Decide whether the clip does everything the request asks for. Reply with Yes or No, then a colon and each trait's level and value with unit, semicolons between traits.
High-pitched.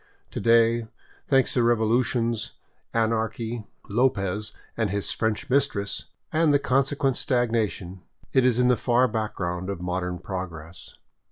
No: low, 115 Hz